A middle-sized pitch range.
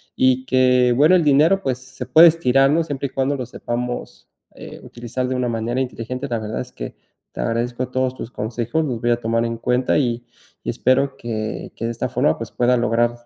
No: narrow, 2.0 semitones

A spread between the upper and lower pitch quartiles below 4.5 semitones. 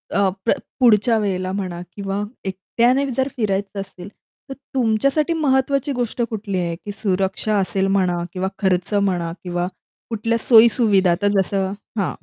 Yes: average, 3.6 semitones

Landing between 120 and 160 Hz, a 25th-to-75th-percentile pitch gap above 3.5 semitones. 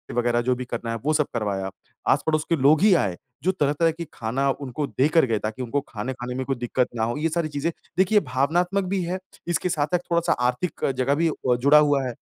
Yes: medium, 140 Hz; average, 5.0 semitones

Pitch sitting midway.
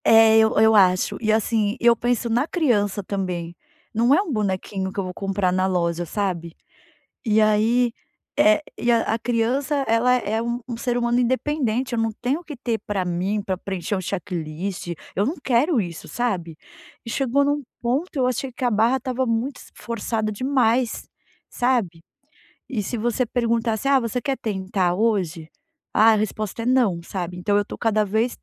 No: high, 225 Hz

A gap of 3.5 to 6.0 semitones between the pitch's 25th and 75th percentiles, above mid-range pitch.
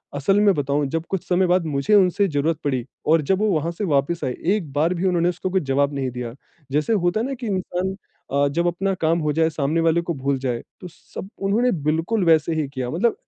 No: average, 4.7 semitones; medium, 165 Hz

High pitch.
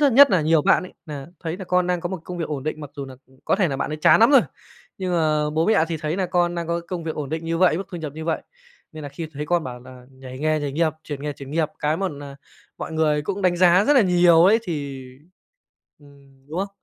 No: medium, 160 Hz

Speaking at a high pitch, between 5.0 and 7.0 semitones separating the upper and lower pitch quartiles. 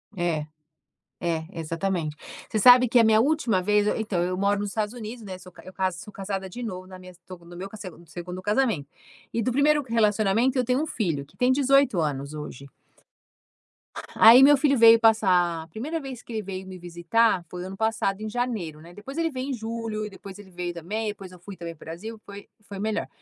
No: high, 205 Hz; average, 4.3 semitones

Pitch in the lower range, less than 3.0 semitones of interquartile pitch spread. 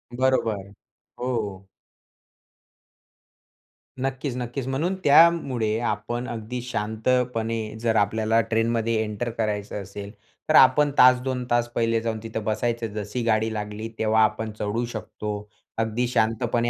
Yes: low, 115 Hz; narrow, 2.4 semitones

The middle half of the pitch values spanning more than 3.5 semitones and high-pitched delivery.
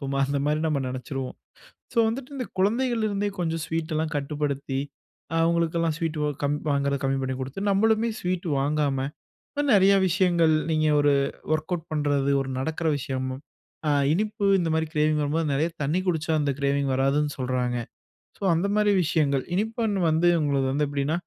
No: average, 3.9 semitones; medium, 155 Hz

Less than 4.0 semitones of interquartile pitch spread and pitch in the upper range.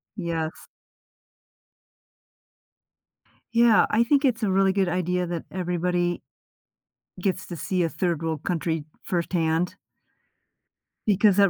No: narrow, 2.5 semitones; medium, 180 Hz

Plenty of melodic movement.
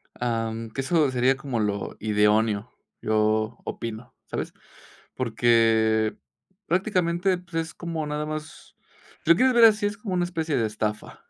Yes: wide, 7.4 semitones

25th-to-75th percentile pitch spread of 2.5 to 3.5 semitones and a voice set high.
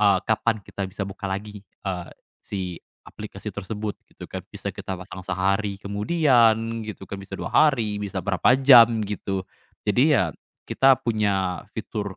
No: average, 2.8 semitones; low, 100 Hz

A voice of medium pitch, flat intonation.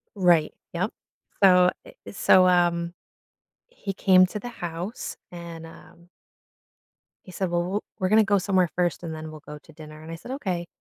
Yes: medium, 175 Hz; narrow, 2.1 semitones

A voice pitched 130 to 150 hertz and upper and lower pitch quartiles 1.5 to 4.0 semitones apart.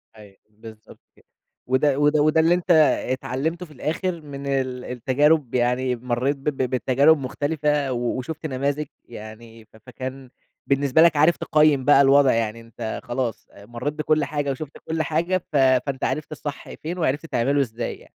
Yes: medium, 140 Hz; average, 3.4 semitones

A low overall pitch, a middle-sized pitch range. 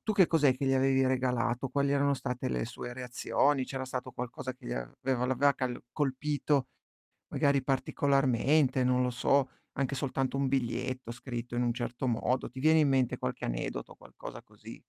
No: low, 130 Hz; narrow, 1.9 semitones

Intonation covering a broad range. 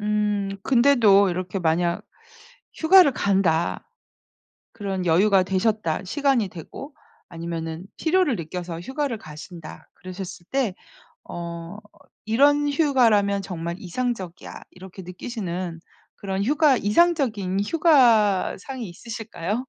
Yes: wide, 5.8 semitones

